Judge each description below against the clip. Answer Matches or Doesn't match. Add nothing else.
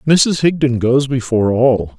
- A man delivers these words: Matches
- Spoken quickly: Doesn't match